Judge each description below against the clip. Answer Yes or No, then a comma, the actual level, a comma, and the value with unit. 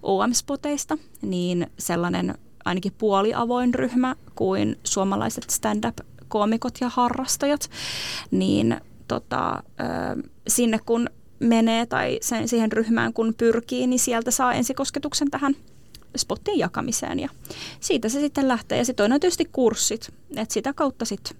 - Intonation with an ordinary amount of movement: Yes, average, 3.9 semitones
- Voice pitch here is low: No, high, 245 Hz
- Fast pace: No, average, 125 wpm